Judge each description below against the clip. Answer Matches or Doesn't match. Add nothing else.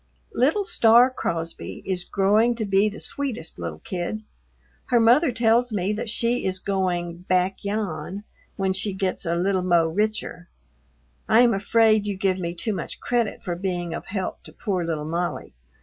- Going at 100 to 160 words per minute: Doesn't match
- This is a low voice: Doesn't match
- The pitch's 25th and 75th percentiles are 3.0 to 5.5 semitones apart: Matches